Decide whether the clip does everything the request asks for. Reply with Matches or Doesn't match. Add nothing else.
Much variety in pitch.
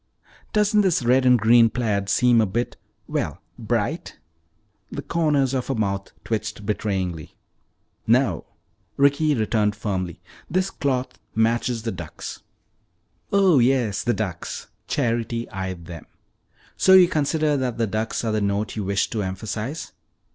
Doesn't match